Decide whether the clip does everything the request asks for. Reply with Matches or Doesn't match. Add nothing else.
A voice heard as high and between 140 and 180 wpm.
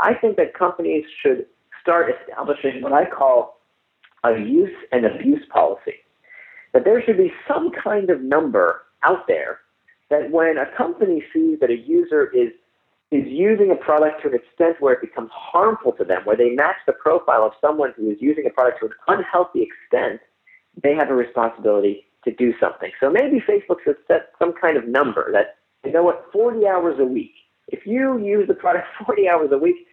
Doesn't match